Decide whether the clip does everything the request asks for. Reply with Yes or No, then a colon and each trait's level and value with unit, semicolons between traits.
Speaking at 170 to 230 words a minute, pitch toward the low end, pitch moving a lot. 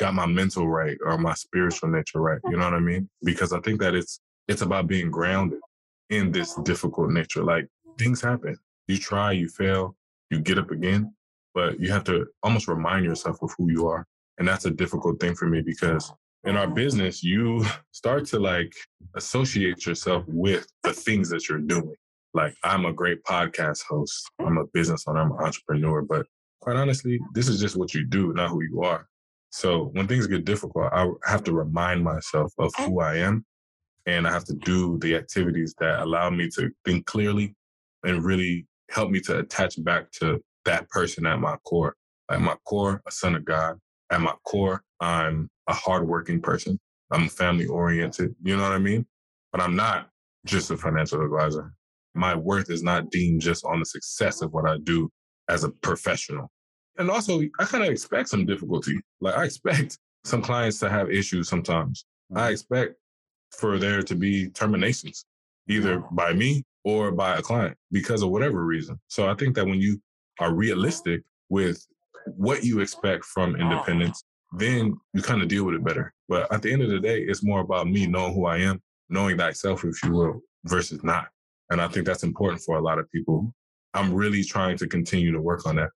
No: average, 195 wpm; very low, 90 Hz; average, 3.5 semitones